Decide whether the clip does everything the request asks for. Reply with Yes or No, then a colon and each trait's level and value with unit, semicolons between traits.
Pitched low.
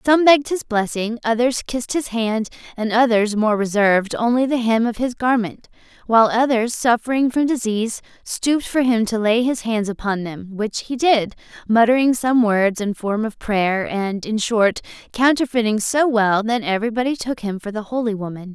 No: high, 225 Hz